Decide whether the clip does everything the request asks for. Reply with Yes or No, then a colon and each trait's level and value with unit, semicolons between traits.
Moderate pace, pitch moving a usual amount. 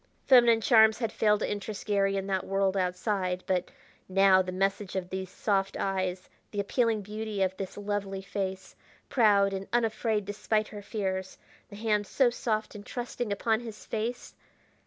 No: average, 165 wpm; narrow, 2.3 semitones